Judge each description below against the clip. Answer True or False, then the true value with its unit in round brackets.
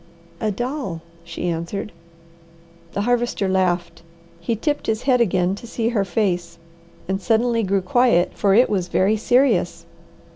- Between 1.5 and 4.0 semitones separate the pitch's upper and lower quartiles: False (4.4 semitones)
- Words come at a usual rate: True (145 wpm)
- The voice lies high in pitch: True (205 Hz)